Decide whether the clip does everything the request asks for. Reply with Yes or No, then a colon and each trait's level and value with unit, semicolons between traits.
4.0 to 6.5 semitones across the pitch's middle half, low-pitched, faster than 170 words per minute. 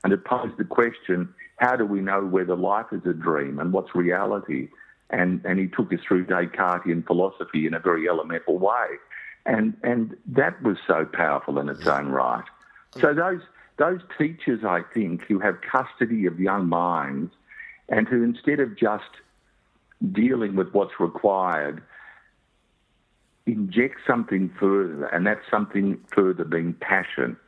No: average, 4.4 semitones; very low, 95 Hz; average, 155 wpm